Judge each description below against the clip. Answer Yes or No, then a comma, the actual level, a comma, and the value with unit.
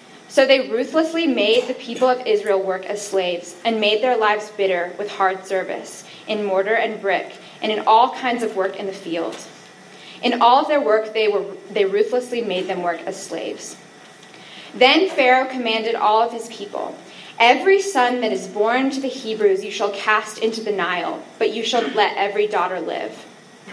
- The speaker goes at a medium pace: Yes, average, 185 wpm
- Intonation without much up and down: No, average, 3.8 semitones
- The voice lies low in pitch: No, high, 220 Hz